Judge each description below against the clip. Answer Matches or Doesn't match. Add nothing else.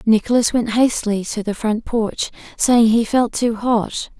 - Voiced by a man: Doesn't match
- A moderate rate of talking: Matches